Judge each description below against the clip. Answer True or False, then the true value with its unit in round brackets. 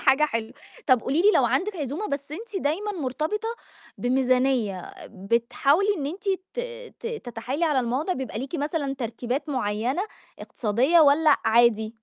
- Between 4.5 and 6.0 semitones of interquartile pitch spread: True (5.2 semitones)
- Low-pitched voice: False (275 Hz)